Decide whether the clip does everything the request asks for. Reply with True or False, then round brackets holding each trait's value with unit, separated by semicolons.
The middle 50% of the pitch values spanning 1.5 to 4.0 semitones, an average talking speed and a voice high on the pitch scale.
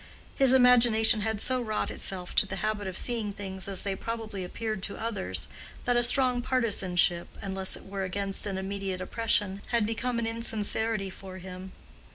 True (3.3 semitones; 175 wpm; 205 Hz)